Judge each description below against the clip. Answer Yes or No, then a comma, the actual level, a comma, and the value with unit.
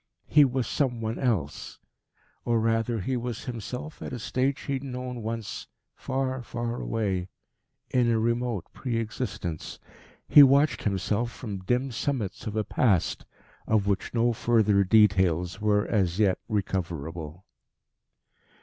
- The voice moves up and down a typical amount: Yes, average, 4.0 semitones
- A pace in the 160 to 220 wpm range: No, average, 140 wpm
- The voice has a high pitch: No, low, 115 Hz